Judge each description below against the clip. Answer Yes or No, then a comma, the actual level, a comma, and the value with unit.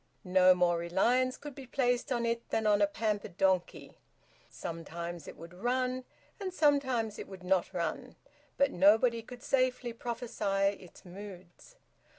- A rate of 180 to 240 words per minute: No, average, 150 wpm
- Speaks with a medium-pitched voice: No, high, 210 Hz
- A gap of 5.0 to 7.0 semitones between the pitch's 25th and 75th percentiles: Yes, wide, 5.5 semitones